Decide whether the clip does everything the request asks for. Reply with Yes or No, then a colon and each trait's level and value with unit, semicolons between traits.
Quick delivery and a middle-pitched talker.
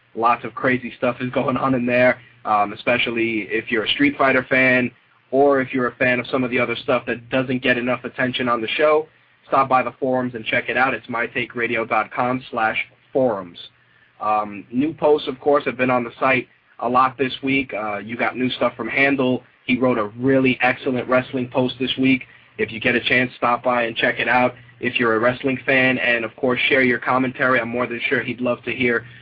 No: fast, 220 wpm; low, 125 Hz